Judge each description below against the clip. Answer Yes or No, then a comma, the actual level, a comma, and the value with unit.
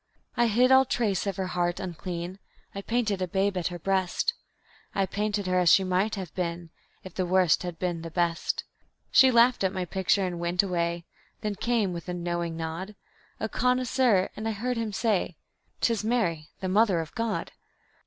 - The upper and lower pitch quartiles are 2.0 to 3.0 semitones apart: No, average, 3.5 semitones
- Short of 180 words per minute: No, average, 190 wpm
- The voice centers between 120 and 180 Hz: No, high, 190 Hz